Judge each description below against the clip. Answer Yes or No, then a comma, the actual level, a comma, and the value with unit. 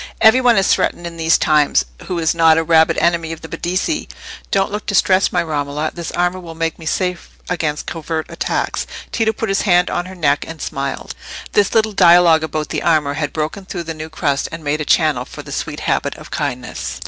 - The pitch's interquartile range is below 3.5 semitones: Yes, average, 2.9 semitones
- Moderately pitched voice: Yes, medium, 165 Hz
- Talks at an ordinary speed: No, fast, 210 wpm